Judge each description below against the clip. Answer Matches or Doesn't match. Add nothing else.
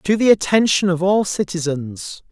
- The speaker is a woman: Doesn't match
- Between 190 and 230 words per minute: Doesn't match